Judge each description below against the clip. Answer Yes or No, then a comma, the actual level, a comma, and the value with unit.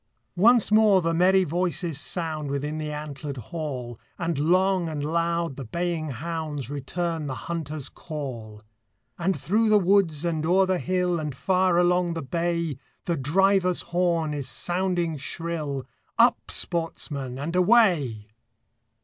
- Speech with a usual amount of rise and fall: Yes, average, 3.6 semitones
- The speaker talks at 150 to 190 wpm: No, average, 140 wpm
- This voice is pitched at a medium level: Yes, medium, 165 Hz